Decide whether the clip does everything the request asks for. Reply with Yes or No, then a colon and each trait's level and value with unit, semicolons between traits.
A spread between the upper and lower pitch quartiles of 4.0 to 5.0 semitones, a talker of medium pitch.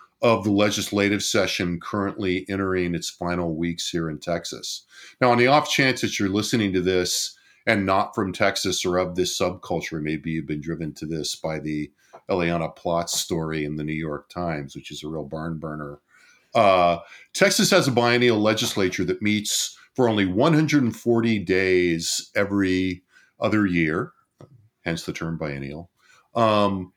No: average, 4.5 semitones; very low, 90 Hz